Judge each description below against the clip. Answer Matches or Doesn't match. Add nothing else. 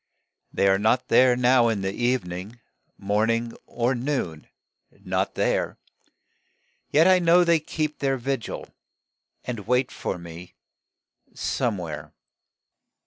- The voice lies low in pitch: Matches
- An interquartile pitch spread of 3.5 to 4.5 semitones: Doesn't match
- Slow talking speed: Matches